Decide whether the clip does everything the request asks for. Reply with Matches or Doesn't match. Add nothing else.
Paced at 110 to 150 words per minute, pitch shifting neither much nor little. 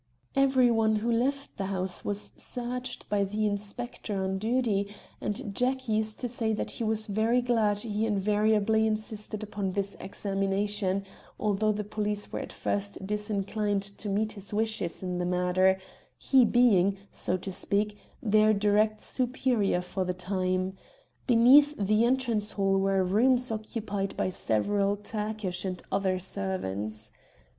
Doesn't match